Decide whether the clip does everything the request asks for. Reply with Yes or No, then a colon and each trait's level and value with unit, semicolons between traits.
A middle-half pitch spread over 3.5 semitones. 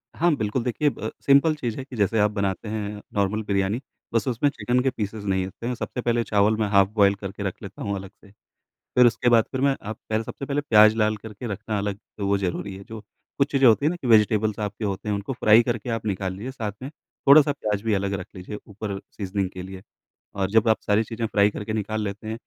No: average, 2.8 semitones